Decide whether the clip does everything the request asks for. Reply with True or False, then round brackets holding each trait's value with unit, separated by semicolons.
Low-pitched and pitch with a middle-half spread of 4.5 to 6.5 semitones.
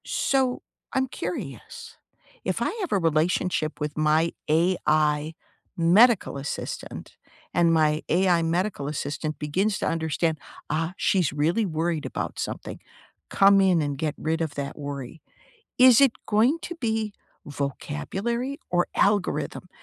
False (165 Hz; 5.1 semitones)